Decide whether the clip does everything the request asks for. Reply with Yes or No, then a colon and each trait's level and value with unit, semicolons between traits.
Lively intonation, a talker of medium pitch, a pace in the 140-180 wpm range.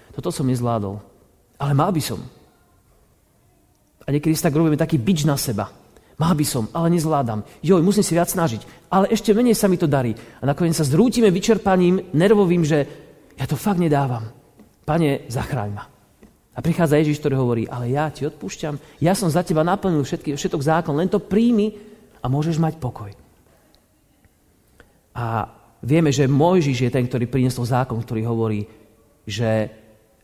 Yes: wide, 6.4 semitones; medium, 145 Hz; fast, 165 wpm